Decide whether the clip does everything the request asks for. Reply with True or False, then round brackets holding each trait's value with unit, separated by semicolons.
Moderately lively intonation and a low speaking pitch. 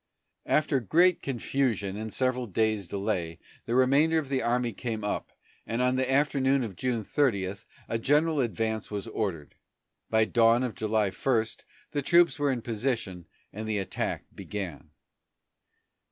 True (4.0 semitones; 115 Hz)